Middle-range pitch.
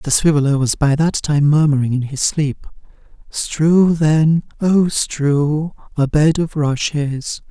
Yes: medium, 150 Hz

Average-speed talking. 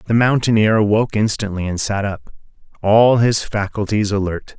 Yes: average, 145 wpm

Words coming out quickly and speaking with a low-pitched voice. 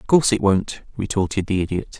Yes: fast, 210 wpm; low, 100 Hz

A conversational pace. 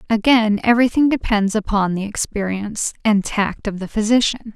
Yes: average, 145 wpm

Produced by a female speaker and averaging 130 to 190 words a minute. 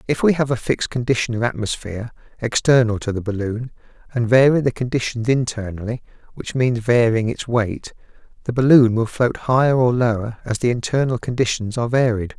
No: male; average, 170 wpm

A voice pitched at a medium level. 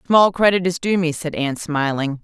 Yes: medium, 165 Hz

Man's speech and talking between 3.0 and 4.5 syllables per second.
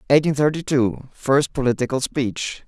Yes: male; 4.4 syllables/s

